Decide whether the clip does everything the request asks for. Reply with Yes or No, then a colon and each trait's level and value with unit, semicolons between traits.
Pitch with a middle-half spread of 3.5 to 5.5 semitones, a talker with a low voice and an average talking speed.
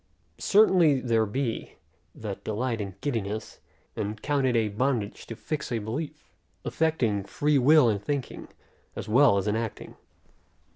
Yes: average, 5.2 semitones; low, 115 Hz; average, 145 wpm